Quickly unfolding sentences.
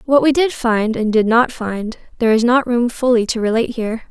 Yes: fast, 235 wpm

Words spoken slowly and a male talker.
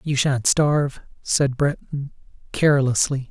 Yes: slow, 110 wpm; male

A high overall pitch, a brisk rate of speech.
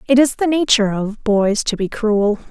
Yes: high, 225 Hz; fast, 215 wpm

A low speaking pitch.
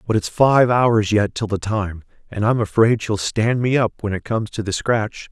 Yes: low, 110 Hz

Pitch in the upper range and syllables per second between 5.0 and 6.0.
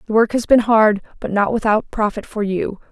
Yes: high, 215 Hz; 5.2 syllables/s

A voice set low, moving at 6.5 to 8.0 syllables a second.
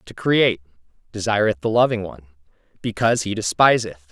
No: low, 105 Hz; 6.0 syllables/s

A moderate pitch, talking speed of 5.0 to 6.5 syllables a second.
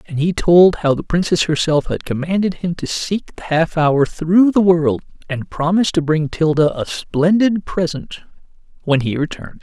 No: medium, 165 Hz; 4.7 syllables/s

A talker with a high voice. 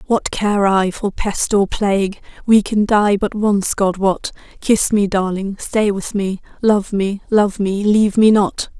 Yes: high, 200 Hz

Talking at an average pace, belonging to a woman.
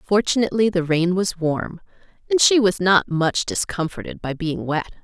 Yes: average, 165 wpm; female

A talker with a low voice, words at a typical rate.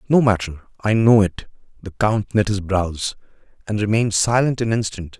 Yes: low, 105 Hz; average, 175 wpm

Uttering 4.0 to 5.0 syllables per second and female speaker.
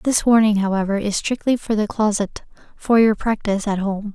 No: 5.2 syllables/s; female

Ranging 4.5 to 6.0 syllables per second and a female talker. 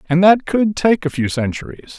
No: 5.0 syllables/s; male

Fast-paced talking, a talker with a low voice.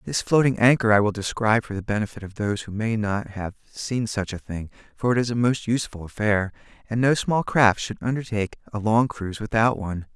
Yes: fast, 220 wpm; low, 110 Hz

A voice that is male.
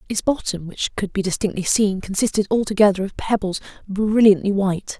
No: female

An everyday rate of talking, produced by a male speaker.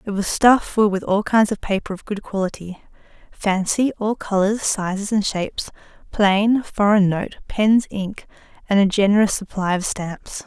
No: average, 160 wpm; female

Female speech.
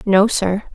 Yes: female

